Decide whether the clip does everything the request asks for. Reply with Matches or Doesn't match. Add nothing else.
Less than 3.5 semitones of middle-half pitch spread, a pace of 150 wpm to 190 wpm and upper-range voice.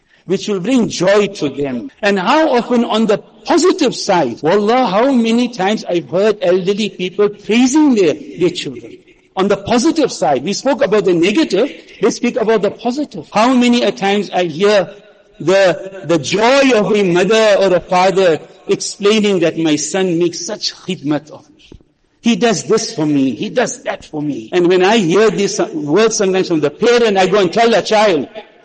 Doesn't match